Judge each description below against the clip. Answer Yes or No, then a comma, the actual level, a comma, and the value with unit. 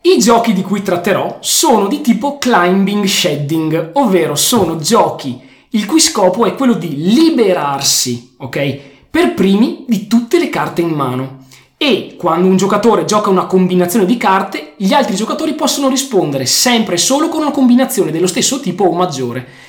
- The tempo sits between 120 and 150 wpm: No, average, 165 wpm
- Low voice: No, high, 190 Hz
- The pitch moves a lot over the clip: Yes, wide, 7.1 semitones